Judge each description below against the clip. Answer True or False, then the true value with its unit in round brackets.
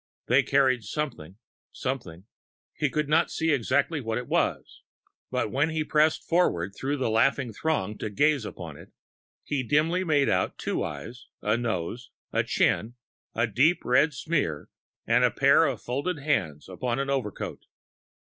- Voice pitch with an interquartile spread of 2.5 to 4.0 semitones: False (5.4 semitones)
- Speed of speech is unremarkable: True (155 wpm)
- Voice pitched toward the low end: True (130 Hz)